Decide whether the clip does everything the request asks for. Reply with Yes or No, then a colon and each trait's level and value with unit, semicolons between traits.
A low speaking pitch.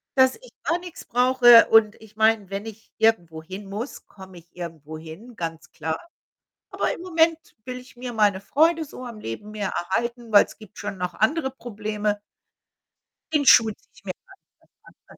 No: high, 220 Hz